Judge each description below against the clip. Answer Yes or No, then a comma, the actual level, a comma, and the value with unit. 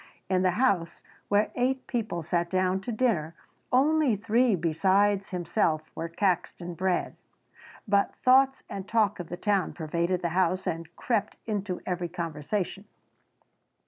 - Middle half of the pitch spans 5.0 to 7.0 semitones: No, average, 3.8 semitones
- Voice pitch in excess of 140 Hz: Yes, high, 190 Hz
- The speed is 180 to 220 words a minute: No, average, 140 wpm